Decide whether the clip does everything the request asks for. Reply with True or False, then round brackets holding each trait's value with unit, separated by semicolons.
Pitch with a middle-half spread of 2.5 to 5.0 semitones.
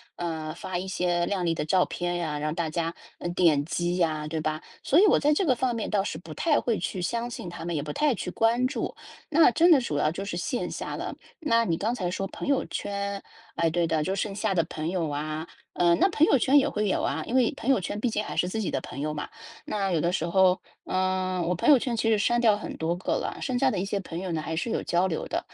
False (5.4 semitones)